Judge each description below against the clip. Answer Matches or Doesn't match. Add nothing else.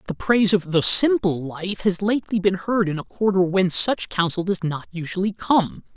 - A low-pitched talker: Doesn't match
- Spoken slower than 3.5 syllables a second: Doesn't match